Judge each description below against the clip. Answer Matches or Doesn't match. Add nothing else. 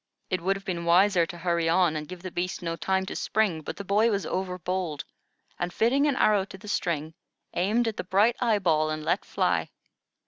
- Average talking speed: Doesn't match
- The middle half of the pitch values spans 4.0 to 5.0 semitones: Doesn't match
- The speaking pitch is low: Doesn't match